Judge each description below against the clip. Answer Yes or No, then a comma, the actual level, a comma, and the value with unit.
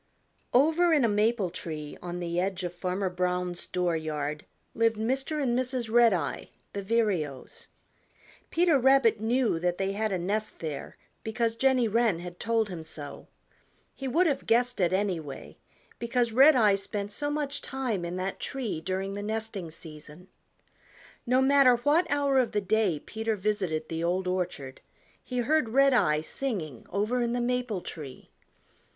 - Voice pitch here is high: Yes, high, 210 Hz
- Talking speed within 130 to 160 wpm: Yes, average, 155 wpm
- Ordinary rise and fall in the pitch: No, wide, 5.7 semitones